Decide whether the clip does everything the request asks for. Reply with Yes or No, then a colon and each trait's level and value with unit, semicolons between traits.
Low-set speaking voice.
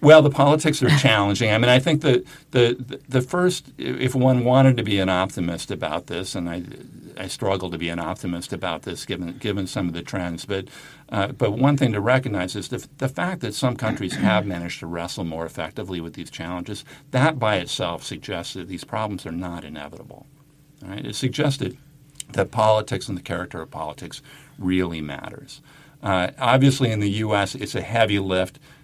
Yes: low, 110 Hz